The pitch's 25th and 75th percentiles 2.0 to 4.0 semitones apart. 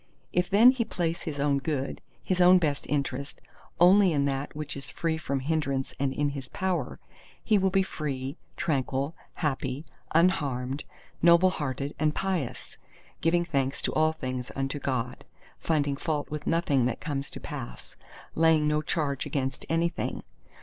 Yes: average, 3.5 semitones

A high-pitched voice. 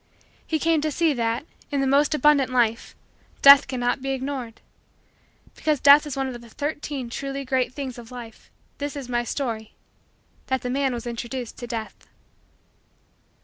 Yes: very high, 265 Hz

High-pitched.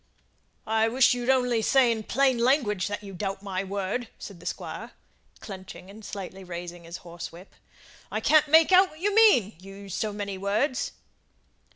Yes: high, 210 Hz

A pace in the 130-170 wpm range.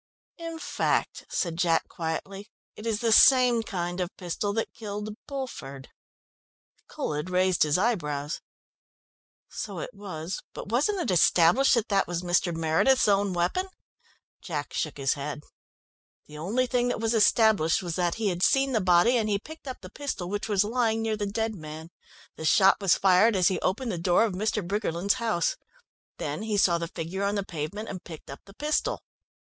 No: average, 180 wpm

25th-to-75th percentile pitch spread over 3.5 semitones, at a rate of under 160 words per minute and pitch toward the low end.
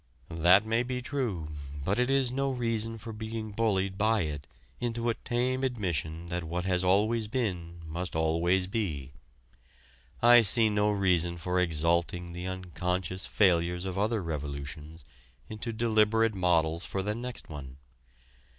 Yes: average, 4.9 semitones; average, 145 wpm; very low, 95 Hz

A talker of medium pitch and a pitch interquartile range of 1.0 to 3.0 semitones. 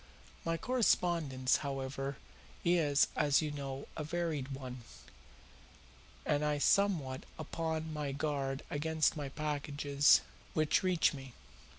Yes: medium, 145 Hz; average, 2.7 semitones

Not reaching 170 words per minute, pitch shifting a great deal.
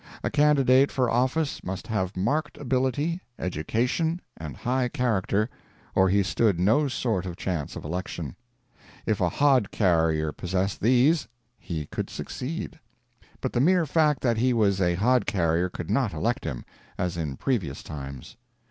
Yes: average, 155 wpm; wide, 6.7 semitones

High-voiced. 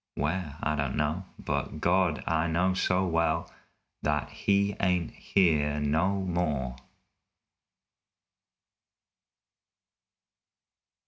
No: very low, 85 Hz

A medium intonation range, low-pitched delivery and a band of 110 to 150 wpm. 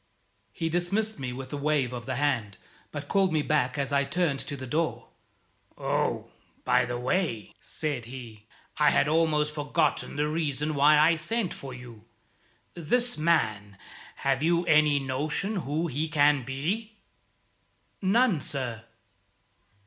No: average, 3.9 semitones; medium, 150 Hz; average, 145 wpm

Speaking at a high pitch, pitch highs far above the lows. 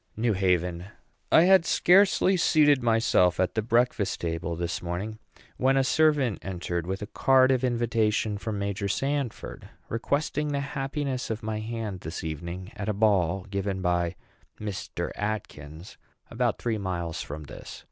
No: low, 105 Hz; wide, 6.2 semitones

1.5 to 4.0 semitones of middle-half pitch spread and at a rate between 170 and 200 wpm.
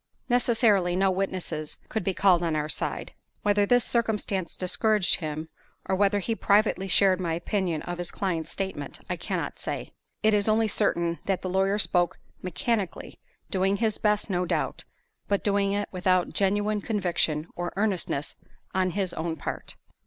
No: average, 2.8 semitones; average, 160 wpm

